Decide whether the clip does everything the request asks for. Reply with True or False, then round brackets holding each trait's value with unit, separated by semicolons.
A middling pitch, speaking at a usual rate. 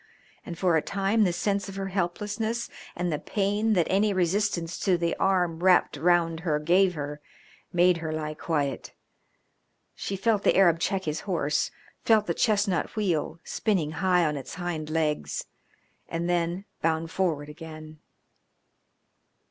True (175 Hz; 150 wpm)